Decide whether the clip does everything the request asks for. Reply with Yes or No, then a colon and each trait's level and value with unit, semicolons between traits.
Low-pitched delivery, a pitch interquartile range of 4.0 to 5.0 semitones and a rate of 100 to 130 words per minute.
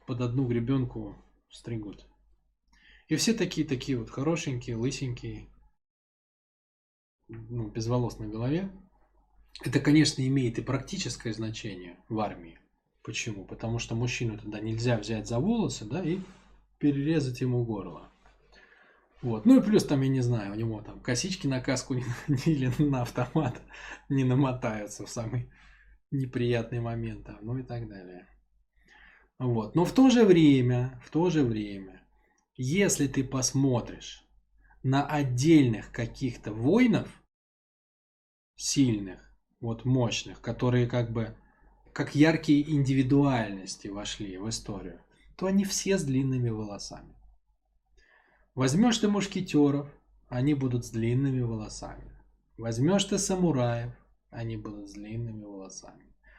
Yes: low, 125 Hz; average, 4.4 semitones; average, 120 wpm